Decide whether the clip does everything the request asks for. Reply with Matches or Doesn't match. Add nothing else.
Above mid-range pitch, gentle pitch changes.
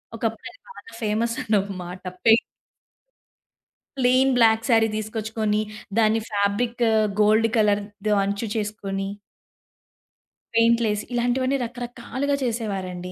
Matches